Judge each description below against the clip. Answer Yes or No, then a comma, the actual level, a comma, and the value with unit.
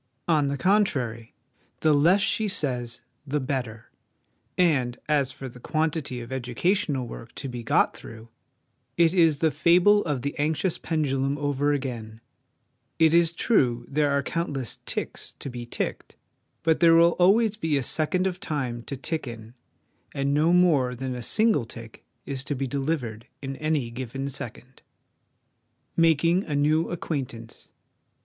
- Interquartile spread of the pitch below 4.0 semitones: No, average, 4.8 semitones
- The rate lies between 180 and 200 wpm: No, average, 155 wpm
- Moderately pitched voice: Yes, medium, 145 Hz